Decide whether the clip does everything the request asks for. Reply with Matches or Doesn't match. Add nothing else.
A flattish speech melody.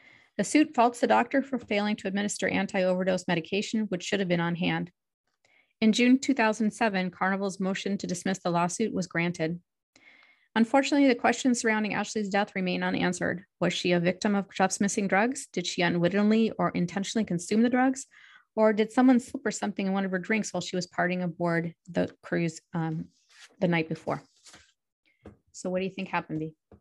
Doesn't match